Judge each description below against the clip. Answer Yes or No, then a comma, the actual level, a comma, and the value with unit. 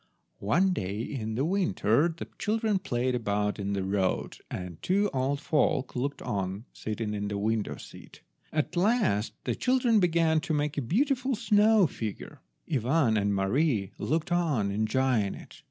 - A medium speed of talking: Yes, average, 160 wpm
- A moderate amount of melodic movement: No, wide, 9.0 semitones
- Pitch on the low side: Yes, low, 130 Hz